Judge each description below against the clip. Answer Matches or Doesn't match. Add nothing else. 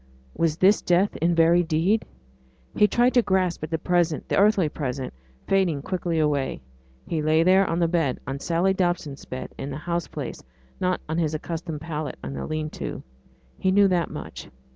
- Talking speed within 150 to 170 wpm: Doesn't match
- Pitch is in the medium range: Matches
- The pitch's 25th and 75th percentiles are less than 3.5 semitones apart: Matches